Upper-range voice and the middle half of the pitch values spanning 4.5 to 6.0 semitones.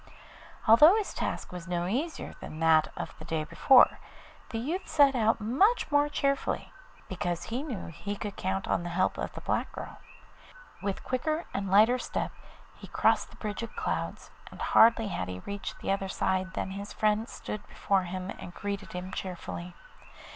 Yes: high, 200 Hz; average, 5.2 semitones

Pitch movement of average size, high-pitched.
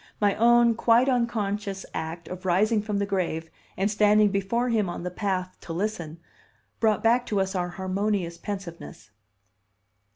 Yes: average, 3.0 semitones; high, 200 Hz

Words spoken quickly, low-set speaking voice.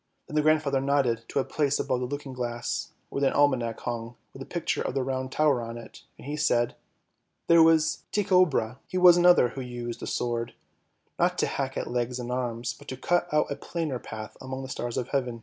Yes: fast, 235 wpm; low, 130 Hz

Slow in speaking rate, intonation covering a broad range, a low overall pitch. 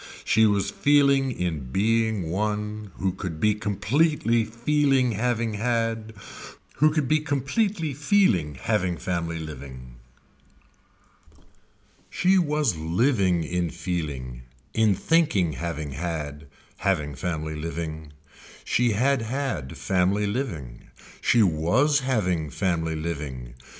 Yes: slow, 110 wpm; wide, 7.5 semitones; low, 100 Hz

